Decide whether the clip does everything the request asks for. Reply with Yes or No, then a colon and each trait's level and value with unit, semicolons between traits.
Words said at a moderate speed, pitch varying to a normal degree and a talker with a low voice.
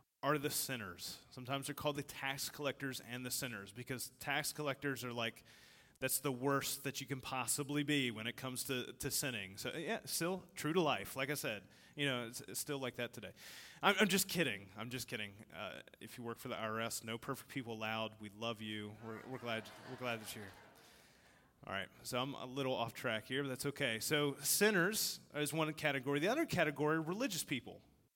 No: fast, 210 wpm; average, 4.0 semitones; low, 130 Hz